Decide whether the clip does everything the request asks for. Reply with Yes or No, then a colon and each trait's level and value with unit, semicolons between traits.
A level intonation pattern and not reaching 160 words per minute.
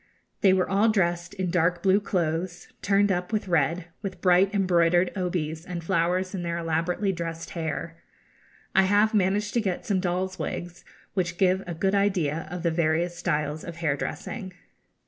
No: narrow, 2.3 semitones; average, 170 wpm